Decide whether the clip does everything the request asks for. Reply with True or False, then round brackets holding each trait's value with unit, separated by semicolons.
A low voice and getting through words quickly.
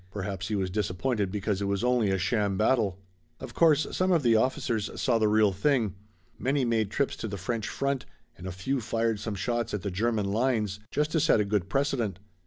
True (110 Hz; 210 wpm)